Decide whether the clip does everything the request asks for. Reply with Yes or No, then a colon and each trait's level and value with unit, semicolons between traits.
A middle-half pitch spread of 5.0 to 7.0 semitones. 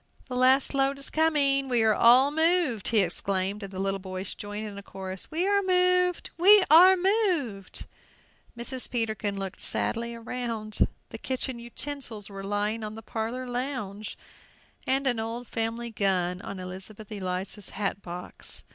Yes: wide, 5.4 semitones